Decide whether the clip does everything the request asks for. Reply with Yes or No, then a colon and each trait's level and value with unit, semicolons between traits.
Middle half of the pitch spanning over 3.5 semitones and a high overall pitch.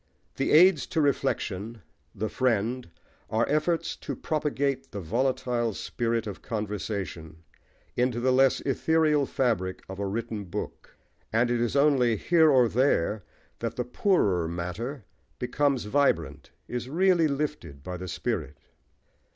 No: wide, 5.6 semitones; low, 120 Hz